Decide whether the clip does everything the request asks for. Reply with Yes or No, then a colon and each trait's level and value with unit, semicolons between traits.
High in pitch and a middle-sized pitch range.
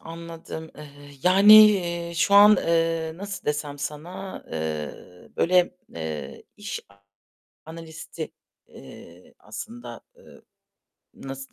No: medium, 165 Hz; average, 5.0 semitones